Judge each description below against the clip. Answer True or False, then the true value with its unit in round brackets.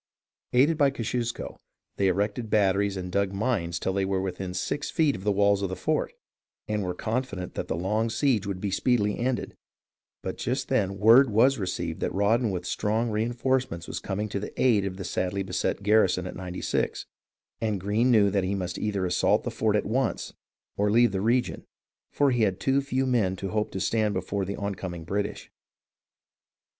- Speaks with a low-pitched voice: True (100 Hz)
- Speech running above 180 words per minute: True (195 wpm)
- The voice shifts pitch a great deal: False (3.4 semitones)